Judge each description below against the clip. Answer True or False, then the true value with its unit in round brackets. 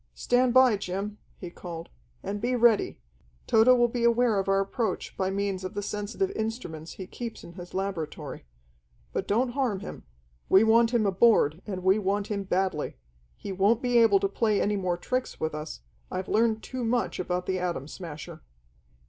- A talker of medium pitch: False (200 Hz)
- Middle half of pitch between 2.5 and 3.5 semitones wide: False (3.9 semitones)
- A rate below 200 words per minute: True (180 wpm)